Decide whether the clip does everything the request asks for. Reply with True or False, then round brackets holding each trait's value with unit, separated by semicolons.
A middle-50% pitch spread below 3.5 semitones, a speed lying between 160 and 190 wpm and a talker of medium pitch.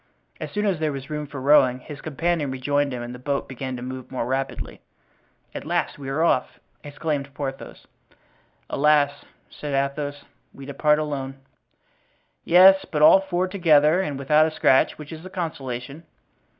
True (2.7 semitones; 165 wpm; 145 Hz)